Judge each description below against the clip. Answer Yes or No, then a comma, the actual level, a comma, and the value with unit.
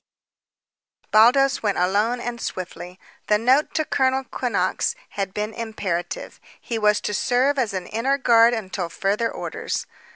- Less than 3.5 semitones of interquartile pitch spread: No, average, 3.8 semitones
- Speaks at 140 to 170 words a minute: Yes, average, 150 wpm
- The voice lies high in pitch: Yes, high, 225 Hz